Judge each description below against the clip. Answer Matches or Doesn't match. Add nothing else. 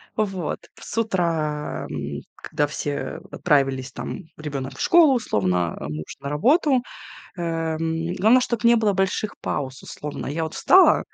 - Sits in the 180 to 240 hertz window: Doesn't match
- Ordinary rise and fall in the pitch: Doesn't match